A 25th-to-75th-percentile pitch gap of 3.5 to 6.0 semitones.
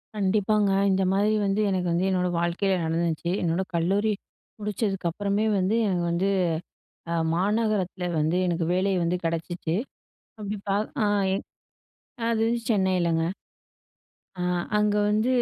No: average, 3.1 semitones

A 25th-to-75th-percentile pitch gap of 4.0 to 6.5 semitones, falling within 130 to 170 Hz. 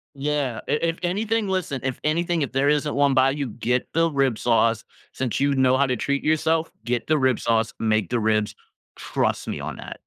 Yes: average, 4.3 semitones; low, 135 Hz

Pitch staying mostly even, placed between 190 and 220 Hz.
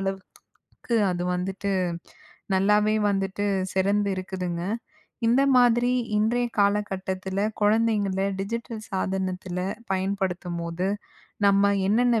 Yes: narrow, 2.1 semitones; high, 195 Hz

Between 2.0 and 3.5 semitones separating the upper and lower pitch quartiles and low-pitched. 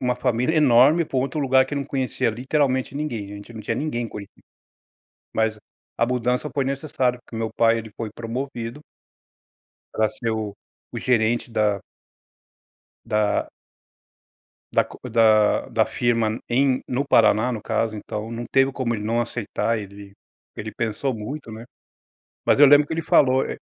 Yes: average, 3.2 semitones; low, 120 Hz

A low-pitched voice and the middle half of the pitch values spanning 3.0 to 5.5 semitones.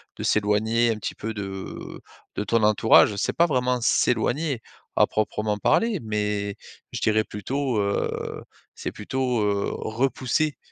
Yes: low, 110 Hz; average, 3.4 semitones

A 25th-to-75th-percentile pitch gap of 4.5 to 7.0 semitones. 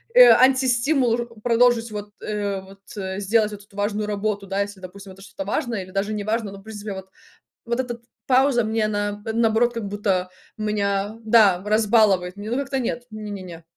No: average, 2.7 semitones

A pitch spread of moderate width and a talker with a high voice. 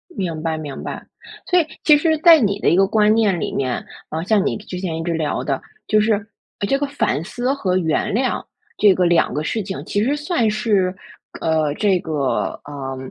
No: wide, 5.8 semitones; high, 195 Hz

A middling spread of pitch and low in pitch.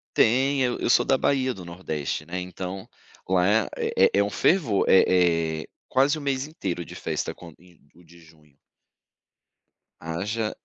No: wide, 7.2 semitones; very low, 95 Hz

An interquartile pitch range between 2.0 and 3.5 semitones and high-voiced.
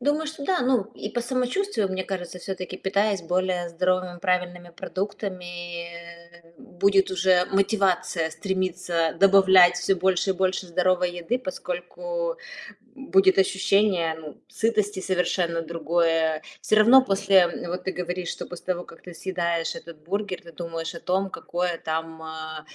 No: narrow, 2.4 semitones; medium, 180 Hz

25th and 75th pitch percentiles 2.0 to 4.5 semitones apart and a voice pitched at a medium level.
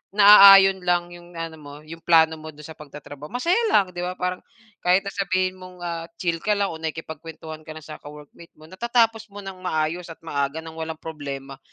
Yes: average, 3.0 semitones; medium, 165 Hz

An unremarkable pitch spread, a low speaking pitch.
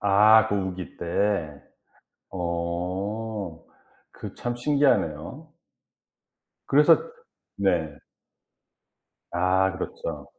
Yes: average, 4.5 semitones; very low, 95 Hz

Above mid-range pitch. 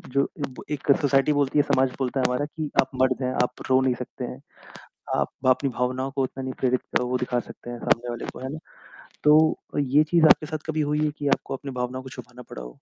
No: low, 130 Hz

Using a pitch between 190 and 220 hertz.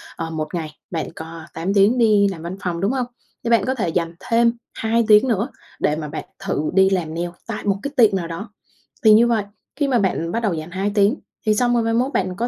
Yes: high, 200 Hz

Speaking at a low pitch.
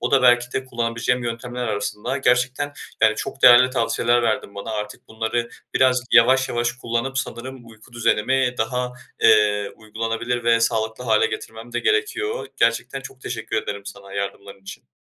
Yes: low, 120 Hz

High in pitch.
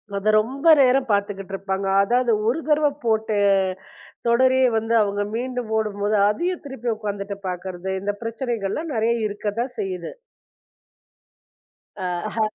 Yes: high, 220 Hz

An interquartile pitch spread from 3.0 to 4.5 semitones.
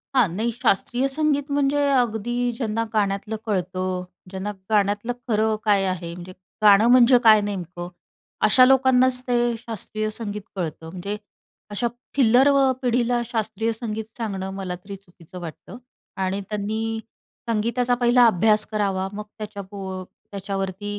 Yes: average, 3.7 semitones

